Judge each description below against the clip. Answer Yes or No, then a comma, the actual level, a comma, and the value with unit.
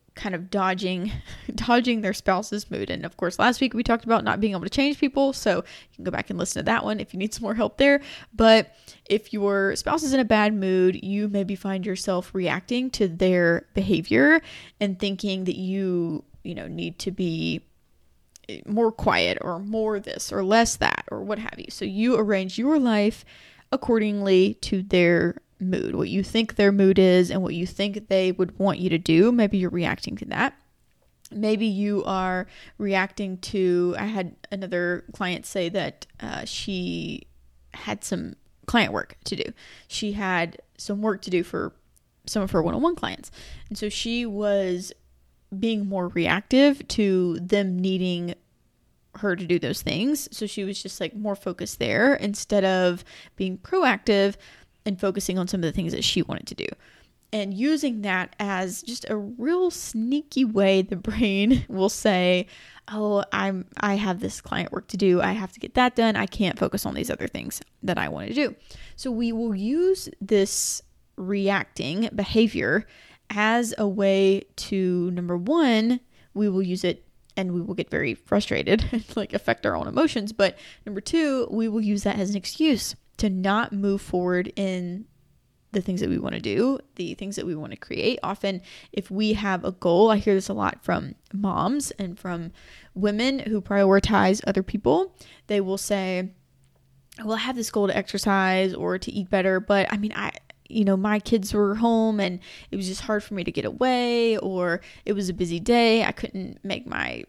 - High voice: Yes, high, 200 Hz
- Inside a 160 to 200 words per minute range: Yes, average, 190 wpm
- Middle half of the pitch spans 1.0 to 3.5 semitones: Yes, average, 3.0 semitones